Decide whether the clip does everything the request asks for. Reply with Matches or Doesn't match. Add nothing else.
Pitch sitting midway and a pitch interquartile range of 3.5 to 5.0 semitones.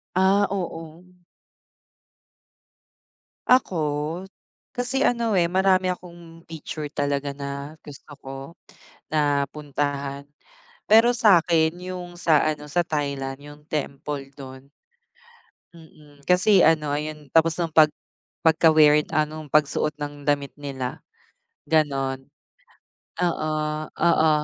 Doesn't match